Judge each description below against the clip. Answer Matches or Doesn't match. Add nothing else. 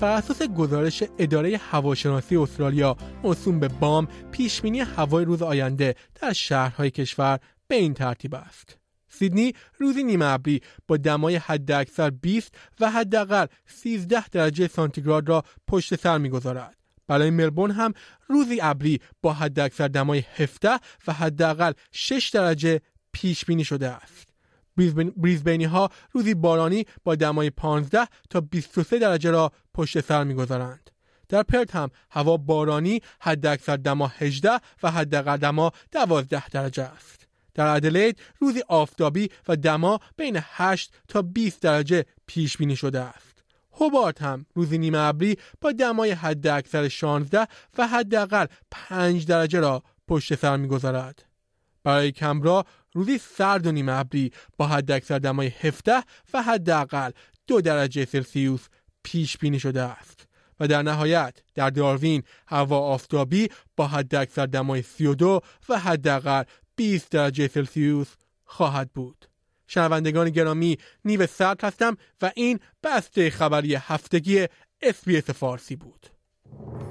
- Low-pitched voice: Doesn't match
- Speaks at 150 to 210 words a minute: Doesn't match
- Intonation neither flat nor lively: Matches